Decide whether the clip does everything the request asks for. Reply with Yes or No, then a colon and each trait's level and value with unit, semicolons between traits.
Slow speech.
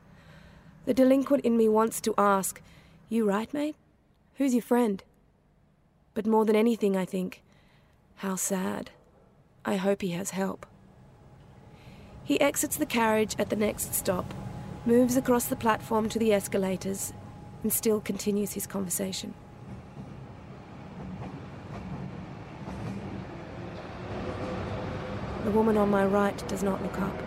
Yes: slow, 120 wpm